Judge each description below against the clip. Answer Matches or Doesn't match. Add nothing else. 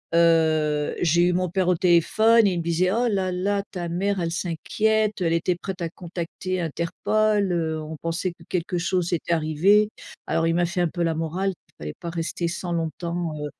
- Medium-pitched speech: Matches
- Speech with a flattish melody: Matches